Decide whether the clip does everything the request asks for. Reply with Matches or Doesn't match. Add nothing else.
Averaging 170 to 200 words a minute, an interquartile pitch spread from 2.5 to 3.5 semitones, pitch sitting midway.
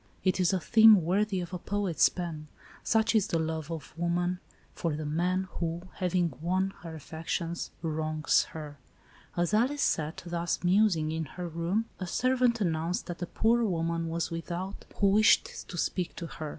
Matches